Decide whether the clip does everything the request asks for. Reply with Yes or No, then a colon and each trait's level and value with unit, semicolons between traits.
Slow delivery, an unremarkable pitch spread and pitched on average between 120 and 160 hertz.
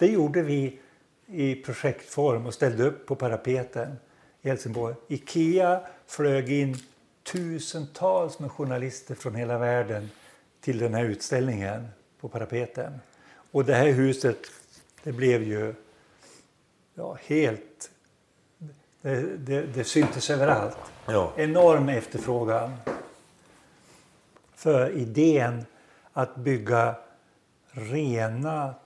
Yes: slow, 100 wpm; average, 3.8 semitones; low, 135 Hz